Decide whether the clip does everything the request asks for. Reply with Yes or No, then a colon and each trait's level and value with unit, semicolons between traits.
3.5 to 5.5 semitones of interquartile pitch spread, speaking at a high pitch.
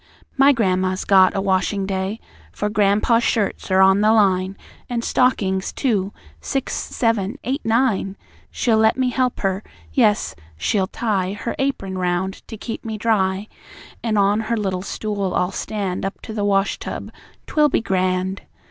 No: average, 3.0 semitones; high, 205 Hz